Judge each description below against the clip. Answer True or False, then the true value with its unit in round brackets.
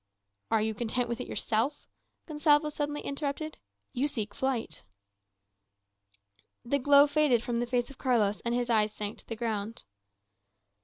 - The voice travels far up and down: False (4.3 semitones)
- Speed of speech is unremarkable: True (150 wpm)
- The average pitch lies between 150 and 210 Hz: False (245 Hz)